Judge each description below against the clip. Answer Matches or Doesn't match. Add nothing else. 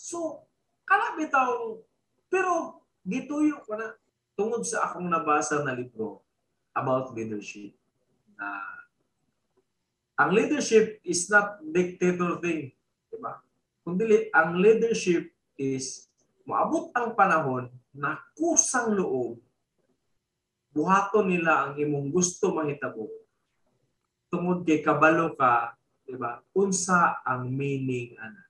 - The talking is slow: Matches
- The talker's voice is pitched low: Doesn't match